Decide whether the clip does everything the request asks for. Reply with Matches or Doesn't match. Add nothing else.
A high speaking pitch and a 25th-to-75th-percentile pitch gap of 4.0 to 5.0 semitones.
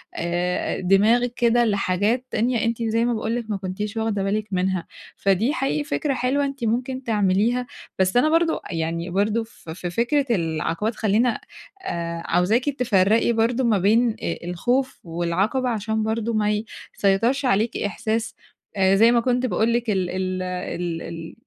Matches